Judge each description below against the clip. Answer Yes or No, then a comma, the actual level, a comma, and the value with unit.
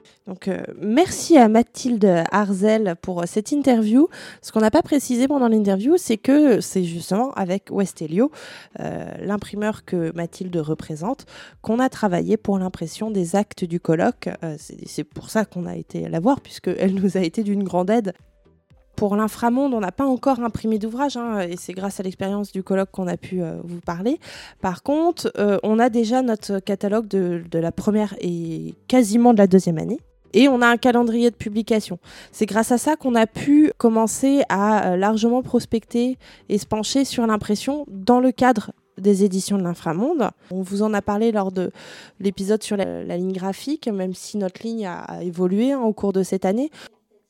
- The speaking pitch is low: No, high, 210 Hz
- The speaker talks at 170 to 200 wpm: Yes, average, 190 wpm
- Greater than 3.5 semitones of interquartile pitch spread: Yes, average, 4.1 semitones